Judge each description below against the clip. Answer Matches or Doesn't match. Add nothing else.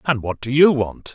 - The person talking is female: Doesn't match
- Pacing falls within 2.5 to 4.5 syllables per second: Doesn't match